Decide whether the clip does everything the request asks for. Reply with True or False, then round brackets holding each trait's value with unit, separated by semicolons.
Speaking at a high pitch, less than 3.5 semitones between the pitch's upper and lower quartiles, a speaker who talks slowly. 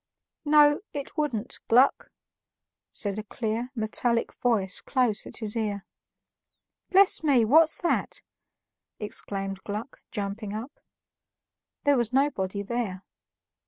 False (230 Hz; 4.8 semitones; 110 wpm)